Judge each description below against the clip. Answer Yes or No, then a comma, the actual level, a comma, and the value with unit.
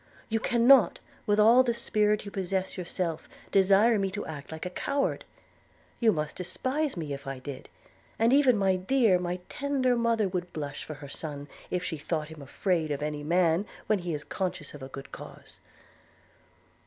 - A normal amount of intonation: No, wide, 6.1 semitones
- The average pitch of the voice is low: No, medium, 185 Hz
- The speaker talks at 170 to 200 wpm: Yes, average, 180 wpm